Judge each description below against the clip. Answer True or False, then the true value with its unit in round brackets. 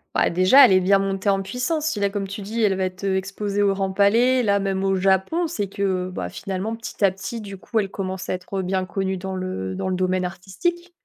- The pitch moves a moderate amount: False (1.7 semitones)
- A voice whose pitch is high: True (195 Hz)